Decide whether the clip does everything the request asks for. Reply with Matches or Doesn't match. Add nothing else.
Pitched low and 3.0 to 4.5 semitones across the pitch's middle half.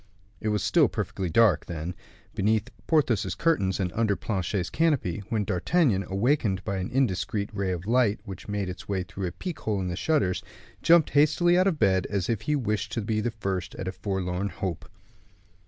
Matches